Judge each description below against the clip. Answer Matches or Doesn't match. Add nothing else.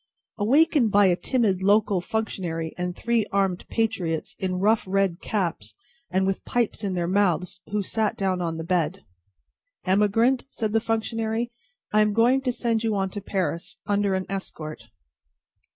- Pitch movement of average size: Matches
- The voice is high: Matches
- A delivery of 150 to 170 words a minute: Matches